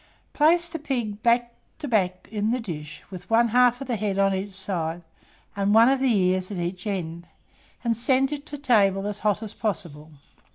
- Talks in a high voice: Yes, high, 210 Hz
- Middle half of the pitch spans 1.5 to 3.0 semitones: No, average, 4.5 semitones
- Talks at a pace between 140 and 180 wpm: No, average, 200 wpm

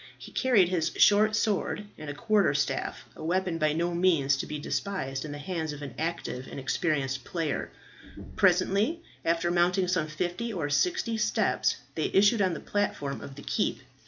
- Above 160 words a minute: Yes, average, 175 wpm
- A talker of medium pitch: Yes, medium, 175 Hz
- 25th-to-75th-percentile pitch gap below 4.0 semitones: No, average, 5.2 semitones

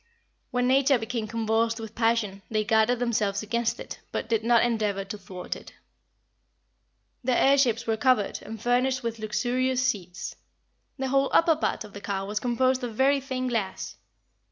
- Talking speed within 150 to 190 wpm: Yes, average, 170 wpm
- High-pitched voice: Yes, high, 230 Hz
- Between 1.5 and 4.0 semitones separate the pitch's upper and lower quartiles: Yes, average, 3.0 semitones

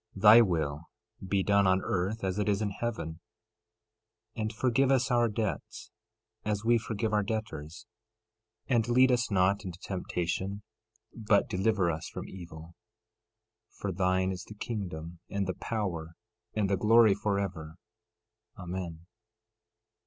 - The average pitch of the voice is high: No, low, 100 Hz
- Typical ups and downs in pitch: Yes, average, 3.5 semitones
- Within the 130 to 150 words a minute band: Yes, average, 145 wpm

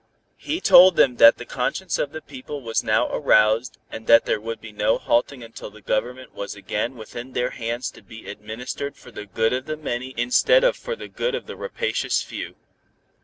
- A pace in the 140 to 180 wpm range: No, fast, 205 wpm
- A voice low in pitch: Yes, low, 125 Hz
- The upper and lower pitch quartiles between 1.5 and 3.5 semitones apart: No, average, 4.0 semitones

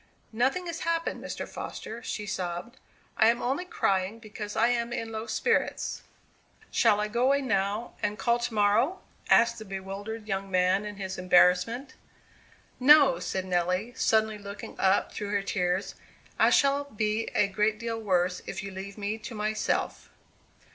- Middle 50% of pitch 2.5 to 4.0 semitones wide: Yes, average, 3.3 semitones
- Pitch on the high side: Yes, high, 215 Hz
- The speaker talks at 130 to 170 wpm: Yes, average, 160 wpm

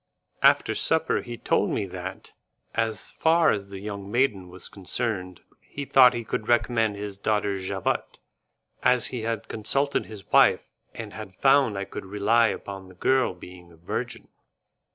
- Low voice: Yes, low, 105 Hz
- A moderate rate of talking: Yes, average, 160 wpm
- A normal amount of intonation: Yes, average, 3.6 semitones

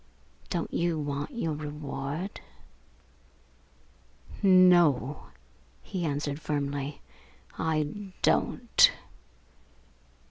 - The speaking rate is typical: No, slow, 65 wpm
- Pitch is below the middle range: No, medium, 150 Hz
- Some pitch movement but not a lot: Yes, average, 3.4 semitones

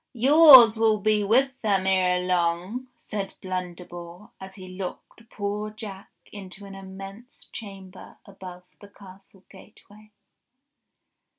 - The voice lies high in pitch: Yes, high, 195 Hz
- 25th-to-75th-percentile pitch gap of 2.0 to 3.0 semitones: Yes, narrow, 2.5 semitones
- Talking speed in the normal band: No, slow, 115 wpm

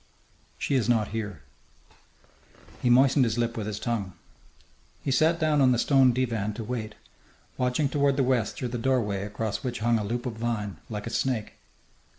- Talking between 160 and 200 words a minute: Yes, average, 180 wpm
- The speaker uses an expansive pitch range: No, average, 3.1 semitones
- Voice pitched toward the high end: No, low, 120 Hz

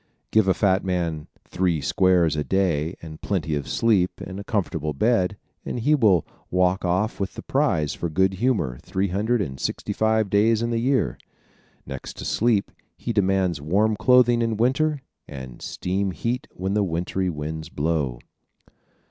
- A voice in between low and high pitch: No, very low, 95 Hz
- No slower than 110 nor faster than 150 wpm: No, average, 165 wpm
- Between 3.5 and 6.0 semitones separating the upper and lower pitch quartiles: Yes, average, 5.2 semitones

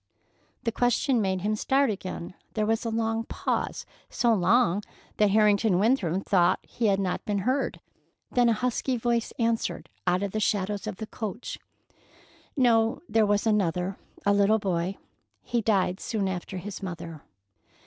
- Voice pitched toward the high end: Yes, high, 210 Hz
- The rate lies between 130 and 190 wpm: Yes, average, 155 wpm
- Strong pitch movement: No, average, 3.3 semitones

